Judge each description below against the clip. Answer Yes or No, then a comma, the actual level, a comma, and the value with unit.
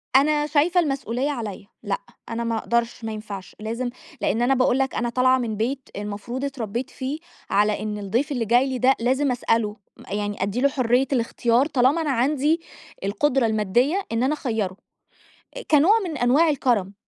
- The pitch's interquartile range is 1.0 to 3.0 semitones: No, average, 3.8 semitones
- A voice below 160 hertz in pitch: No, high, 245 Hz